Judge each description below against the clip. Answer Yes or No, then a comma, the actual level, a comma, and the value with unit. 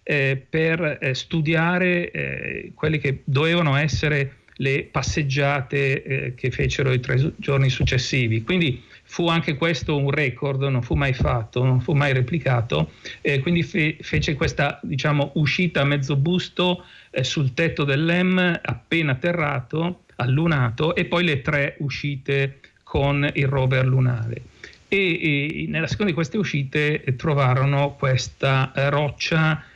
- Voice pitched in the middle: Yes, medium, 145 Hz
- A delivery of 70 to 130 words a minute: Yes, average, 125 wpm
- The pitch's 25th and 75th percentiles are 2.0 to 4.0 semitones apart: Yes, average, 3.5 semitones